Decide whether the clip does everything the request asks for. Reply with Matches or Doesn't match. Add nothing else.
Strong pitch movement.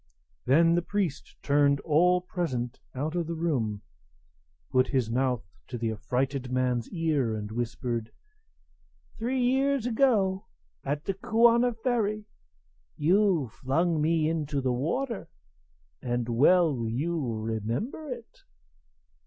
Matches